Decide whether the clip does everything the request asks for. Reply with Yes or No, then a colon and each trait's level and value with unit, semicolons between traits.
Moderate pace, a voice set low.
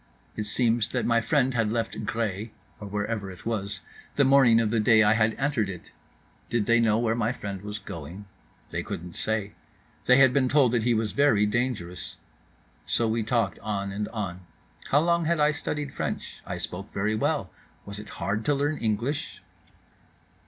Yes: average, 175 wpm; low, 110 Hz